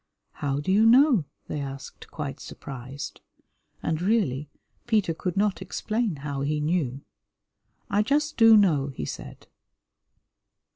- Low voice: No, medium, 165 Hz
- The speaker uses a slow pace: Yes, slow, 130 wpm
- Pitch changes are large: Yes, wide, 7.3 semitones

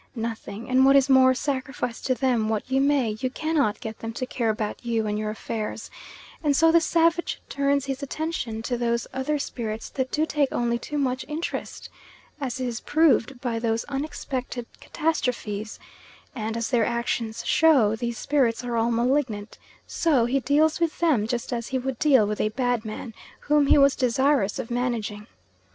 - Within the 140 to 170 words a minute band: No, average, 180 wpm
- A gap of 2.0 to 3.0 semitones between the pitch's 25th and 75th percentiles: No, average, 3.5 semitones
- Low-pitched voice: No, very high, 250 Hz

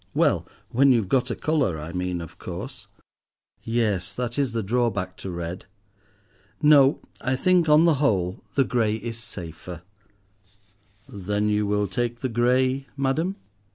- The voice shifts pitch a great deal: Yes, wide, 5.8 semitones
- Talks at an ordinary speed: Yes, average, 150 wpm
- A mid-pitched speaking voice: No, low, 115 Hz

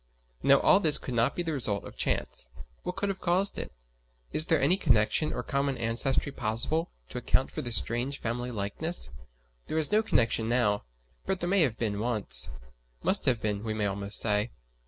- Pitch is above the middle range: No, low, 120 Hz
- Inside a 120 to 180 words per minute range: No, average, 195 wpm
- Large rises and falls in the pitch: Yes, wide, 6.6 semitones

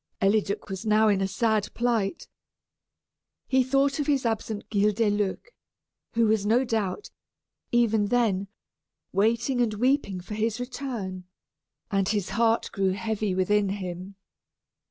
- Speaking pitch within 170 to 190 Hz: No, high, 215 Hz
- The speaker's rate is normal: No, slow, 130 wpm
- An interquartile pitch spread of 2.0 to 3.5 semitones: Yes, average, 3.1 semitones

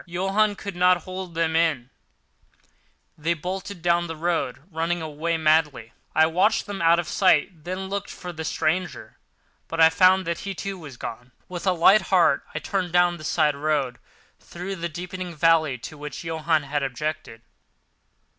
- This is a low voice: No, medium, 165 Hz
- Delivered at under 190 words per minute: Yes, average, 170 wpm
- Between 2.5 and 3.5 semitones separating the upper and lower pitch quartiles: Yes, average, 2.8 semitones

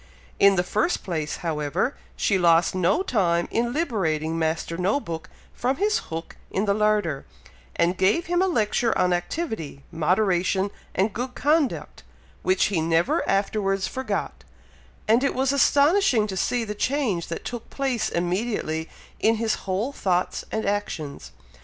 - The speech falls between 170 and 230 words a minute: No, average, 150 wpm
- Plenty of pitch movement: Yes, wide, 6.1 semitones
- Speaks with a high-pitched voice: Yes, high, 200 Hz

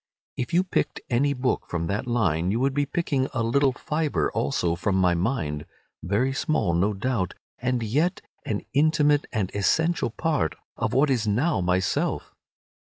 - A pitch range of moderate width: No, wide, 7.1 semitones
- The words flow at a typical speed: Yes, average, 160 wpm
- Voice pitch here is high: No, low, 120 Hz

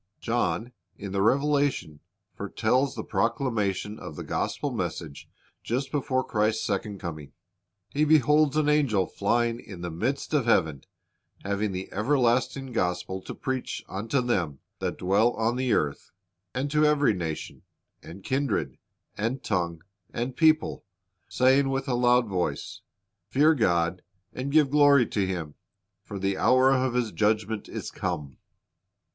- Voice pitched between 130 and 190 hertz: No, low, 115 Hz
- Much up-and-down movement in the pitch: Yes, wide, 5.8 semitones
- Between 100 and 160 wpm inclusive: Yes, average, 140 wpm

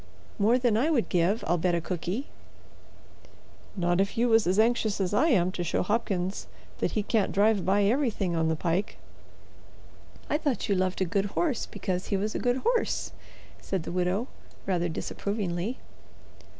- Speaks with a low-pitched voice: No, high, 200 Hz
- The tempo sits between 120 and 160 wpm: No, average, 175 wpm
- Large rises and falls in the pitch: No, average, 4.1 semitones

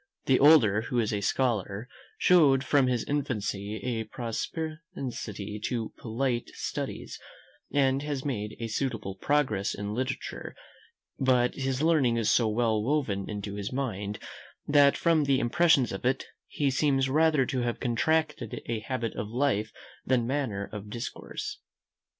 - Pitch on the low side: Yes, low, 125 Hz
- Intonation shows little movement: No, average, 4.5 semitones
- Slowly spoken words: No, average, 145 wpm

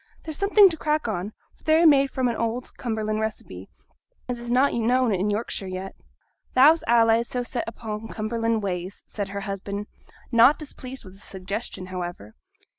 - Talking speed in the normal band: Yes, average, 175 wpm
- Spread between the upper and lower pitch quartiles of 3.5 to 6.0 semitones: Yes, average, 4.2 semitones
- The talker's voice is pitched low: No, high, 225 Hz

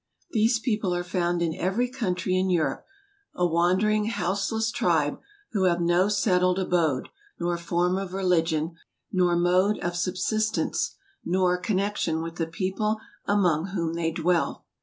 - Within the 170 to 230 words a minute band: No, average, 145 wpm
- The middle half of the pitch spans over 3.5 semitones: No, narrow, 2.5 semitones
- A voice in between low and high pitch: Yes, medium, 180 Hz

